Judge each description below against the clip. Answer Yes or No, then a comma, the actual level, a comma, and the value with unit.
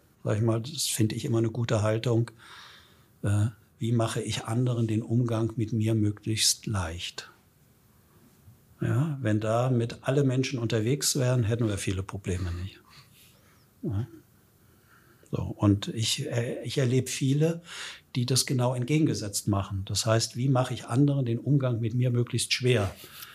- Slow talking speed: No, average, 150 wpm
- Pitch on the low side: Yes, low, 115 Hz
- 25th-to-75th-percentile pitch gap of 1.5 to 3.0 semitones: Yes, narrow, 2.6 semitones